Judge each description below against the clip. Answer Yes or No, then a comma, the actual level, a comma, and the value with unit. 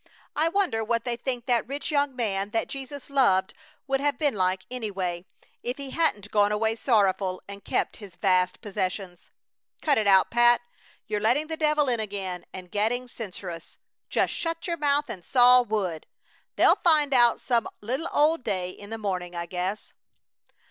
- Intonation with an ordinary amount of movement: No, wide, 5.9 semitones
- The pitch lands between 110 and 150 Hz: No, high, 225 Hz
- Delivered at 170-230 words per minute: Yes, average, 175 wpm